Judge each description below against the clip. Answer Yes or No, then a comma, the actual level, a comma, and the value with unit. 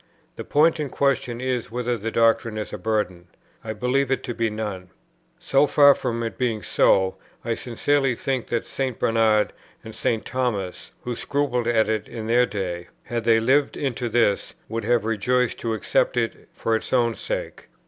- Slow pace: No, average, 180 wpm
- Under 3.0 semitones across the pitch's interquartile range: Yes, narrow, 2.4 semitones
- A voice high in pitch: No, low, 115 Hz